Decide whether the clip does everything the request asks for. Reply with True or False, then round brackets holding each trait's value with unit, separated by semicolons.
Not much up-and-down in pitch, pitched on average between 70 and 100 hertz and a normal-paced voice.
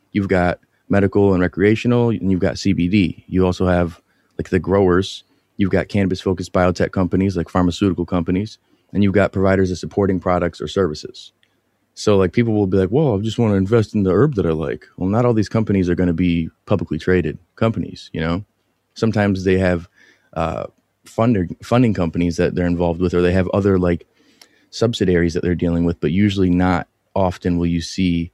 True (2.3 semitones; 95 Hz; 195 wpm)